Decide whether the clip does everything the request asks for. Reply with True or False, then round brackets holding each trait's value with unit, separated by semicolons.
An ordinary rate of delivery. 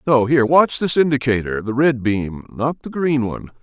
True (165 wpm)